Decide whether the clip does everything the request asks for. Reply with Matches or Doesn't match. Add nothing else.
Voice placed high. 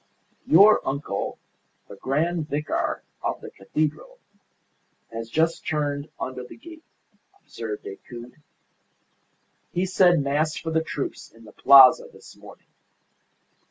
Doesn't match